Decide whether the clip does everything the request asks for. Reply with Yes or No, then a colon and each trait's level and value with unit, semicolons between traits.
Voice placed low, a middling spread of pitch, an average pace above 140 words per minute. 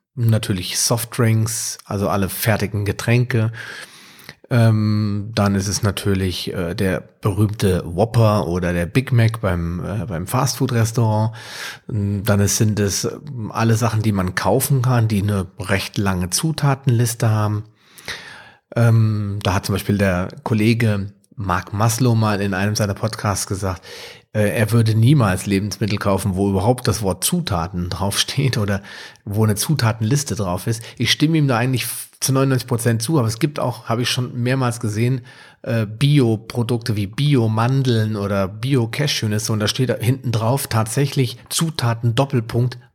No: low, 110 Hz; average, 3.3 semitones; average, 135 wpm